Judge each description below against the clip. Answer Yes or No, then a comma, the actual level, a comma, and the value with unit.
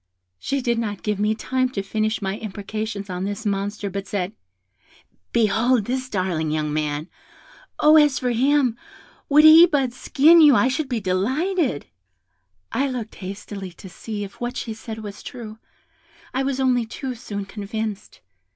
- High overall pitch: Yes, high, 220 Hz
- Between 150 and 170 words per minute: Yes, average, 160 wpm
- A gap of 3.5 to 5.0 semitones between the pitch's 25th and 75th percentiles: Yes, average, 4.6 semitones